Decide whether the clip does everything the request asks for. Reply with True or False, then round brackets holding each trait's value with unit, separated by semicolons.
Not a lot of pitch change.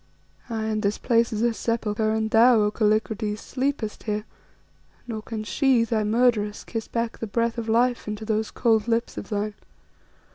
True (1.6 semitones)